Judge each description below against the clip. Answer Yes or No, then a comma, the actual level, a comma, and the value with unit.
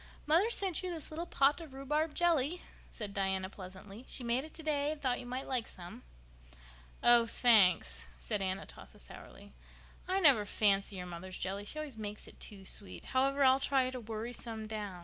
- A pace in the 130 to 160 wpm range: No, average, 185 wpm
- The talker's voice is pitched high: Yes, high, 240 Hz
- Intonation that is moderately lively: No, wide, 6.6 semitones